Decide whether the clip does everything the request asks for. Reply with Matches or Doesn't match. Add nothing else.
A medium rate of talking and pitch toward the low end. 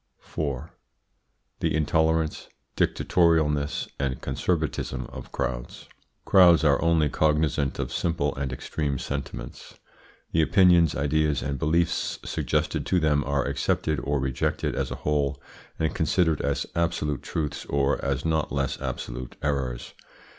Doesn't match